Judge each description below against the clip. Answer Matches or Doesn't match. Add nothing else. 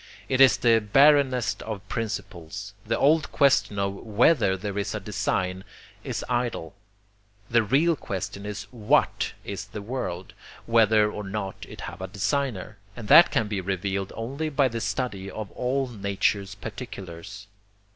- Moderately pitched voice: Doesn't match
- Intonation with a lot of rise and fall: Doesn't match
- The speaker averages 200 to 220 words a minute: Doesn't match